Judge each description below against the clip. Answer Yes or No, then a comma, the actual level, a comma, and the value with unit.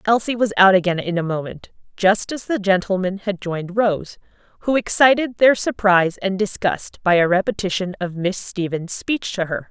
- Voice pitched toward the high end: Yes, high, 195 Hz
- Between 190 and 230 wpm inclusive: No, average, 180 wpm